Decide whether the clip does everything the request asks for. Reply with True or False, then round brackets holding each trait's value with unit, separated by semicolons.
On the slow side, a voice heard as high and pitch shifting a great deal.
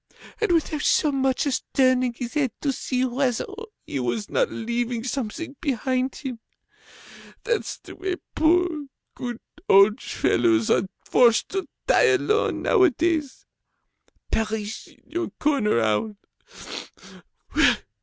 True (120 wpm; 260 Hz; 5.7 semitones)